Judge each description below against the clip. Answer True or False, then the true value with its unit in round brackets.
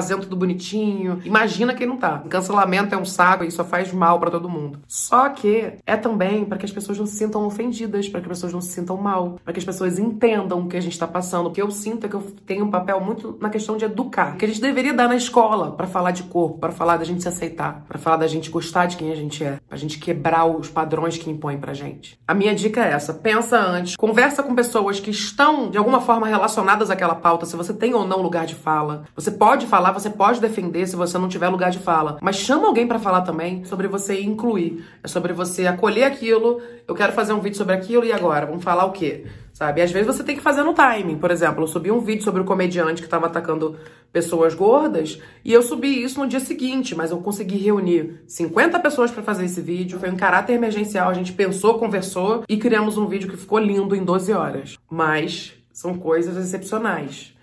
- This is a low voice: False (190 Hz)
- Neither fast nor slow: False (240 wpm)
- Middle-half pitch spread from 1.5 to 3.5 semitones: False (4.1 semitones)